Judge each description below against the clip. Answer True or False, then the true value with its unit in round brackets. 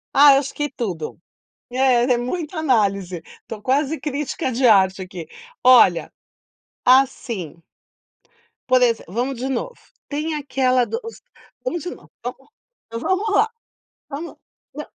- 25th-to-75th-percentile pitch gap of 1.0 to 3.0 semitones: False (4.7 semitones)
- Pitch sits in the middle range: False (255 Hz)